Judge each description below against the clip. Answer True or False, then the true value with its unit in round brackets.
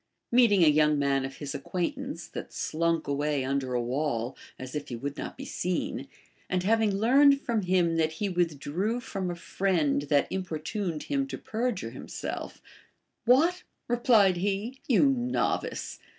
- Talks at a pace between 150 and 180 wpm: True (165 wpm)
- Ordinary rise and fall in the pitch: False (7.5 semitones)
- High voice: False (180 Hz)